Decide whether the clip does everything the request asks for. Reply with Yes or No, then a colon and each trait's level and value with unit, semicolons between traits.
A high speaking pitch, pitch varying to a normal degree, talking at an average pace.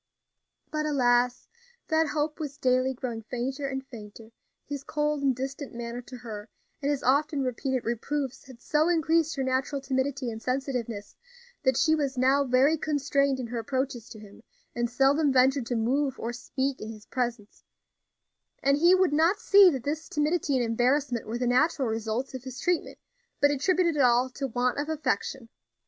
Yes: very high, 265 Hz; average, 3.1 semitones; average, 175 wpm